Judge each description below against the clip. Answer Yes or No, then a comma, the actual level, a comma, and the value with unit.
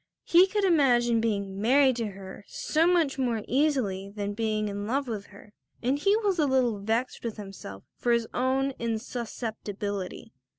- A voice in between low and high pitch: No, high, 235 Hz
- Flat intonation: No, average, 4.7 semitones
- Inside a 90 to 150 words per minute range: No, average, 165 wpm